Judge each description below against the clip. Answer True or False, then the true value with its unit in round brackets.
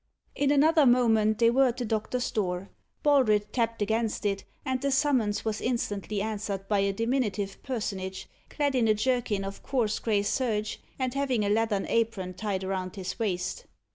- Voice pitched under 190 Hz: False (220 Hz)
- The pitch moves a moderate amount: True (3.8 semitones)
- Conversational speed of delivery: True (170 wpm)